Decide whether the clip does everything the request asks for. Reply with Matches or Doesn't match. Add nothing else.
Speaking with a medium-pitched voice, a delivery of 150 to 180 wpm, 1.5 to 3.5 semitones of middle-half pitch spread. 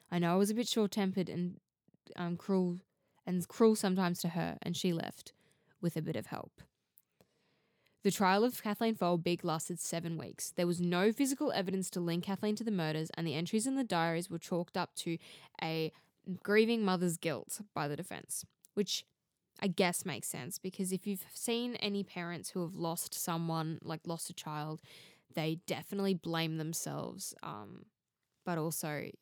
Matches